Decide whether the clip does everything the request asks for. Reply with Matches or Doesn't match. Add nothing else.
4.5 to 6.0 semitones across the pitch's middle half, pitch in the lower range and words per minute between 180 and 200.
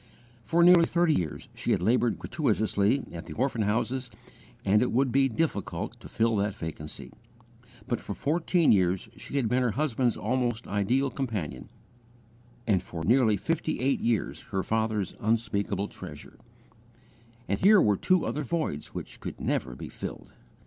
Doesn't match